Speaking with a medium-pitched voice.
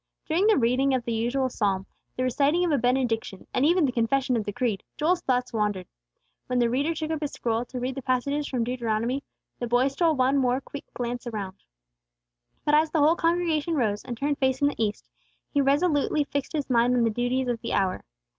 No: very high, 255 Hz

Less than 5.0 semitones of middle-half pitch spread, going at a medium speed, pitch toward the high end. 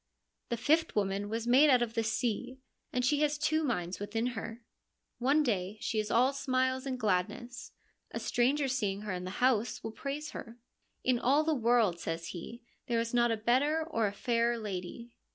Yes: average, 3.4 semitones; average, 195 wpm; high, 235 Hz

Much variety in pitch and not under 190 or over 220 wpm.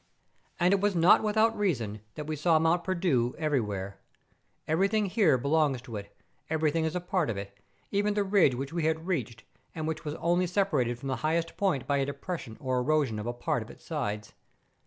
Yes: wide, 6.1 semitones; average, 200 wpm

